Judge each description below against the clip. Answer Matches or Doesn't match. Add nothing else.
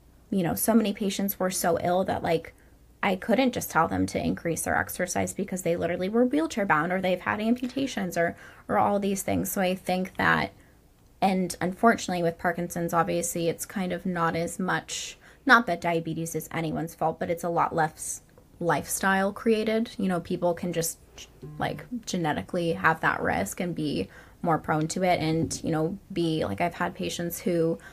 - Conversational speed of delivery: Matches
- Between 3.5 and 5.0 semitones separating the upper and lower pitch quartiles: Doesn't match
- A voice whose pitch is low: Doesn't match